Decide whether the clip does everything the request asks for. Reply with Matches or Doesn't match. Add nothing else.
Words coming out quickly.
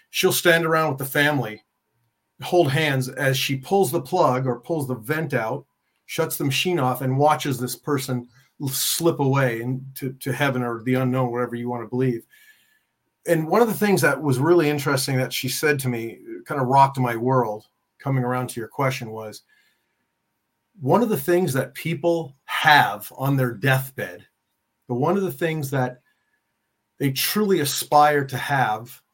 Doesn't match